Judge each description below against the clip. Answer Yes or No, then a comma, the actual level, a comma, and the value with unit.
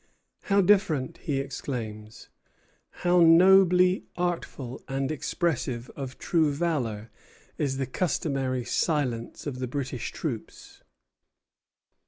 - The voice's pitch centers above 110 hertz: Yes, medium, 140 Hz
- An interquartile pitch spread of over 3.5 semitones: Yes, average, 5.1 semitones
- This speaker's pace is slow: Yes, slow, 100 wpm